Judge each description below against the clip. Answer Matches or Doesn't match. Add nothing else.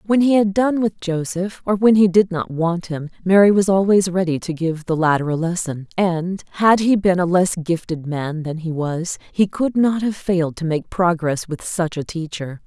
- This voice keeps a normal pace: Doesn't match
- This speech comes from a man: Doesn't match